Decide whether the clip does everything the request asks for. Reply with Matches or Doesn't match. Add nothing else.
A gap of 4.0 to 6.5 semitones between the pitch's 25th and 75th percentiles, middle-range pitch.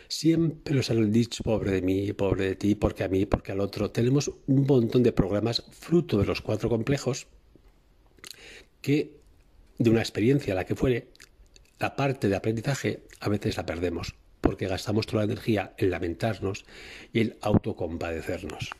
Doesn't match